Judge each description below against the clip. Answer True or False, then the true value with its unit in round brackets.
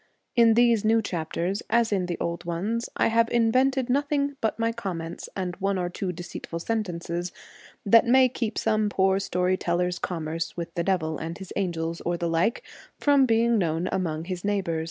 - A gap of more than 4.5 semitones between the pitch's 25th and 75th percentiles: True (4.9 semitones)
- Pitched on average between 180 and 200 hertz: True (190 Hz)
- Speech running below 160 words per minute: False (180 wpm)